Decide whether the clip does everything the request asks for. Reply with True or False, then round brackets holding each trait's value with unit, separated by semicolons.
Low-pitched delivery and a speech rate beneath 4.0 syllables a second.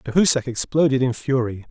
False (130 Hz; 5.5 syllables/s)